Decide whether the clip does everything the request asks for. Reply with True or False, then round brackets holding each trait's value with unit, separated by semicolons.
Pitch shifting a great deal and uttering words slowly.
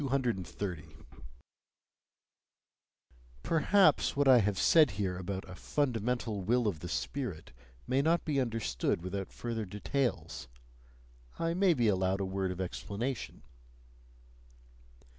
True (6.3 semitones; 115 wpm)